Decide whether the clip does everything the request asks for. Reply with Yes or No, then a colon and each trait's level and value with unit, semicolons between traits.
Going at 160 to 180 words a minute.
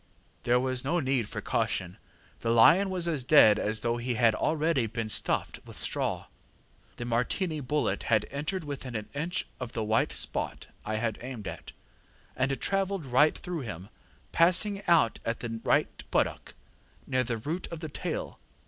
Yes: average, 170 wpm